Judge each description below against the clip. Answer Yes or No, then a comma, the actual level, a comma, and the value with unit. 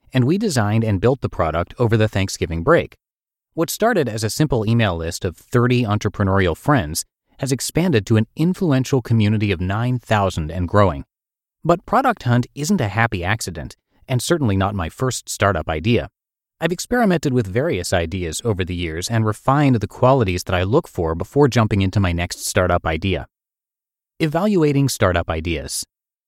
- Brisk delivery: No, average, 165 wpm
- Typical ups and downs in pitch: No, wide, 6.0 semitones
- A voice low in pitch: Yes, low, 110 Hz